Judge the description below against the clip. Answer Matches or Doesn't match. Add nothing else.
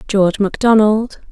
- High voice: Matches